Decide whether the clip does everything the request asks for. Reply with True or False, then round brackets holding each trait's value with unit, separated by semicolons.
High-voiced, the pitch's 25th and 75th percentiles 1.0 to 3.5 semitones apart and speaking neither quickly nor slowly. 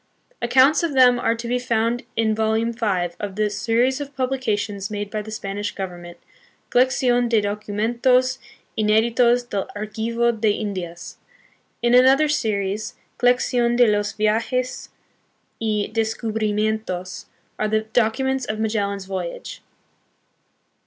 False (220 Hz; 2.9 semitones; 130 wpm)